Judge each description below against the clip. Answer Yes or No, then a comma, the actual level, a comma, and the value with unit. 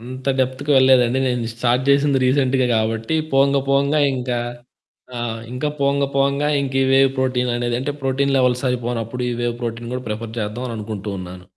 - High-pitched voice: No, low, 125 Hz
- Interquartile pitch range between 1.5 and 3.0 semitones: Yes, narrow, 2.5 semitones